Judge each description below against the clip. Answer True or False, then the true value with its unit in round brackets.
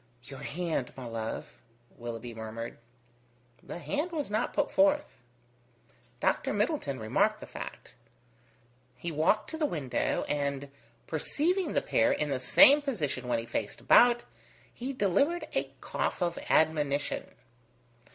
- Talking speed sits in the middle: False (130 wpm)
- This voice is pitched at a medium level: True (160 Hz)